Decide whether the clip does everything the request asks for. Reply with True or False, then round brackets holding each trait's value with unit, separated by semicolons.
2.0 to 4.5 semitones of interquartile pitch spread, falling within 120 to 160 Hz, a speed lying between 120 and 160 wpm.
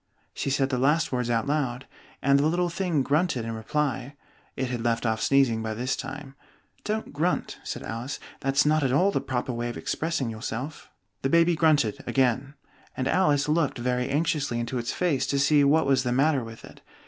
False (3.6 semitones; 135 Hz; 195 wpm)